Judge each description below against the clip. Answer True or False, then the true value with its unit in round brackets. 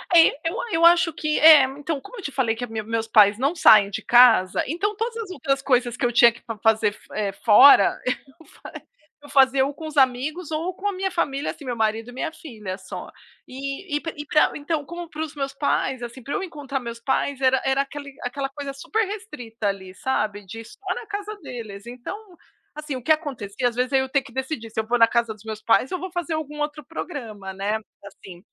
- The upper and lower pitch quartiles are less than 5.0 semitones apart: False (5.5 semitones)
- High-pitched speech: True (270 Hz)